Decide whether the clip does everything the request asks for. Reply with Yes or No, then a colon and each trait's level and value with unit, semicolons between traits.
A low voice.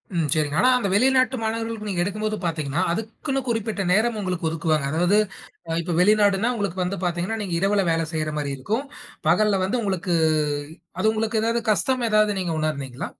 No: high, 200 Hz